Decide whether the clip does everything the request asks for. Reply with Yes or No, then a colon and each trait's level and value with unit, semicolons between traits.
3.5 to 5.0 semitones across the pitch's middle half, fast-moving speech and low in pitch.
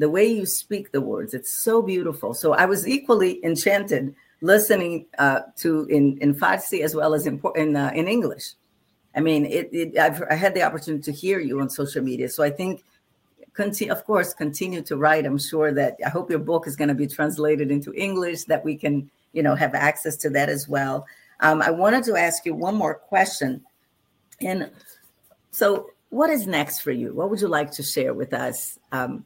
No: average, 4.5 semitones; fast, 210 wpm; medium, 155 Hz